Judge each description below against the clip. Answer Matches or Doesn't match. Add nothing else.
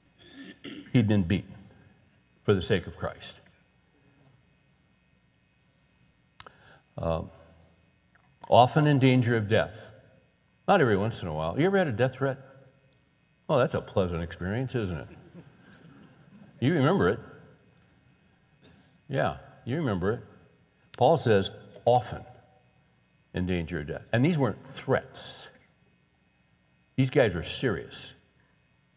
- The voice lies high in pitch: Doesn't match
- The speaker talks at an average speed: Doesn't match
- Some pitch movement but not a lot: Doesn't match